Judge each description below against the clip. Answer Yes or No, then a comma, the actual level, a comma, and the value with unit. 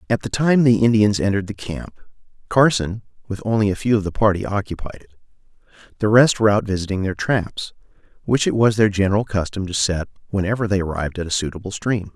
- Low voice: Yes, low, 105 Hz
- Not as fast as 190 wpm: No, average, 200 wpm